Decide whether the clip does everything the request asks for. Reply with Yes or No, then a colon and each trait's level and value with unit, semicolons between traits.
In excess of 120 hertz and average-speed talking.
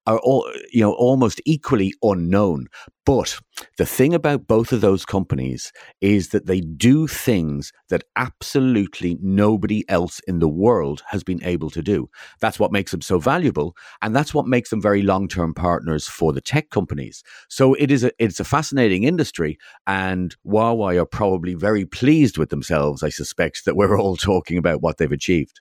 No: low, 100 Hz; average, 180 wpm